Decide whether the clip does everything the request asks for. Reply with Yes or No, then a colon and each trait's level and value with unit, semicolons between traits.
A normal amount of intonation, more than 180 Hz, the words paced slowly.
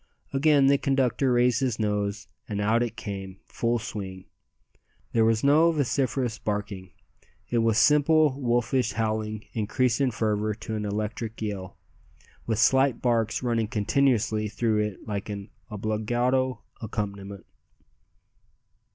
No: average, 3.2 semitones; low, 110 Hz; slow, 125 wpm